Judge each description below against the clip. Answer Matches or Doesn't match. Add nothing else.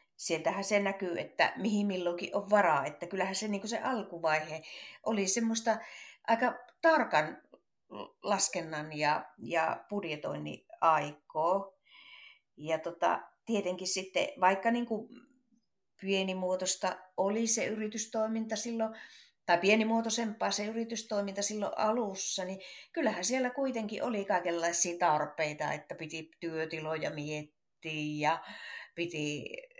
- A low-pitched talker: Doesn't match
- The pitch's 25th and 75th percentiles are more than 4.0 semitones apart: Matches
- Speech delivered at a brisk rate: Doesn't match